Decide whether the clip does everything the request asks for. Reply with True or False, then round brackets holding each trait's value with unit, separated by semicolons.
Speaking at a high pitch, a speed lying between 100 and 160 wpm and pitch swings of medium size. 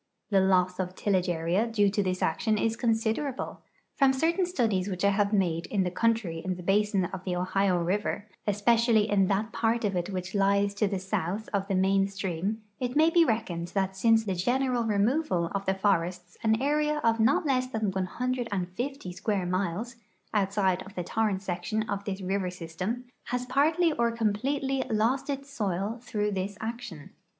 False (205 Hz; 185 wpm; 3.7 semitones)